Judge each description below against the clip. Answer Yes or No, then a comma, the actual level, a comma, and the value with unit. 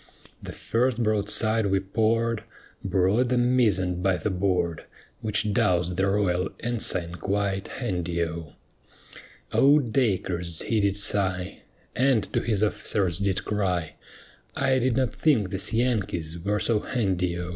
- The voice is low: Yes, low, 100 Hz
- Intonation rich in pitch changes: No, average, 4.0 semitones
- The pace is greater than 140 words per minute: No, slow, 135 wpm